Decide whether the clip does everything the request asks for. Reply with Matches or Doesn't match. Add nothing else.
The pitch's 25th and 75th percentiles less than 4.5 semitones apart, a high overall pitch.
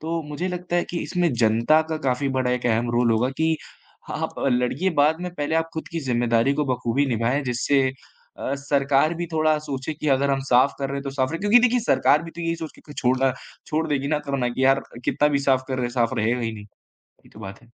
Doesn't match